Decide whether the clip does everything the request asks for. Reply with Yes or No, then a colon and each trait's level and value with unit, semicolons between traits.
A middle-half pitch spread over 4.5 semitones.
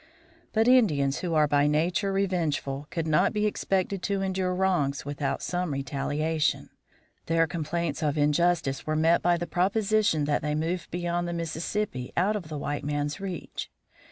No: average, 3.9 semitones